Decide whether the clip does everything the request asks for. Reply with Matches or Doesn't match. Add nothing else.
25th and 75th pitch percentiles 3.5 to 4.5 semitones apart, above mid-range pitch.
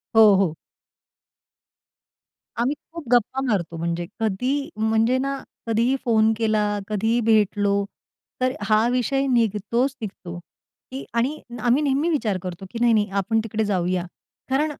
Matches